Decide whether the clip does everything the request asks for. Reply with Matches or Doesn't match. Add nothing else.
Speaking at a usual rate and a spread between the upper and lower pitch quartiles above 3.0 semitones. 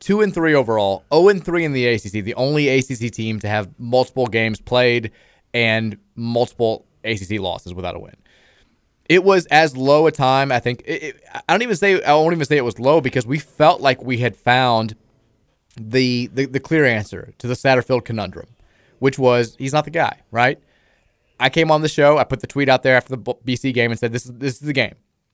Doesn't match